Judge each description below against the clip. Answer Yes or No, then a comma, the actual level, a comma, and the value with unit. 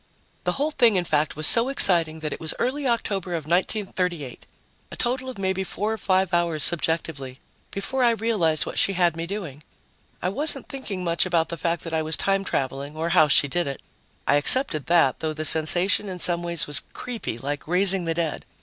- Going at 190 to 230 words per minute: Yes, fast, 205 wpm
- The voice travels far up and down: No, average, 4.1 semitones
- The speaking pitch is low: No, medium, 175 Hz